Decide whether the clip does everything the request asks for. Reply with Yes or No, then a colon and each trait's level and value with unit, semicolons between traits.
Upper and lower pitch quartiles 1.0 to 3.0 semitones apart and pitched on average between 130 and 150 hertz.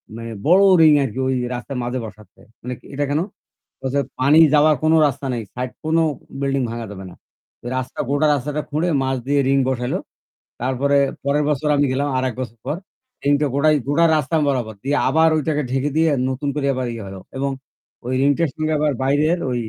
Yes: narrow, 2.6 semitones; medium, 140 Hz